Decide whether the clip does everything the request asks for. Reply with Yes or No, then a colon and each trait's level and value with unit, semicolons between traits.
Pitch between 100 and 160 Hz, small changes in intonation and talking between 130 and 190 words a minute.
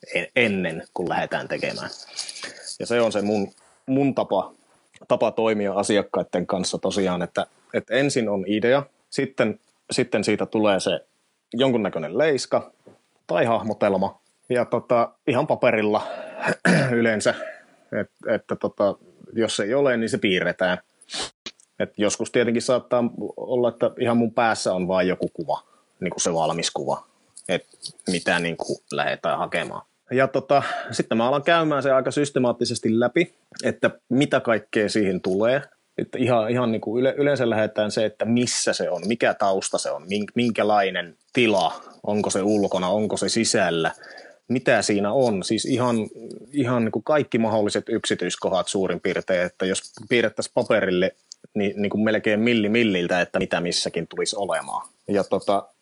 No: low, 110 Hz; average, 3.5 semitones; average, 150 wpm